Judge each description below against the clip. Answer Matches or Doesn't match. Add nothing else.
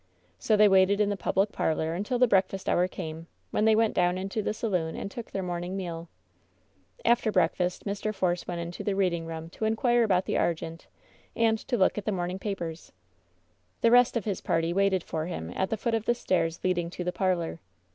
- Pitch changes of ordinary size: Matches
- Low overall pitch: Doesn't match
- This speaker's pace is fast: Matches